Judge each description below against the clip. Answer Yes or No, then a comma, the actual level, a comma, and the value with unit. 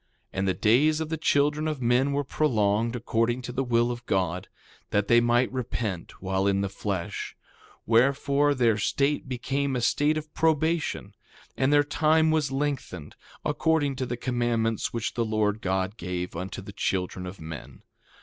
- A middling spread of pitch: No, wide, 5.8 semitones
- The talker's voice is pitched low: Yes, low, 120 Hz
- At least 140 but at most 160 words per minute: No, average, 170 wpm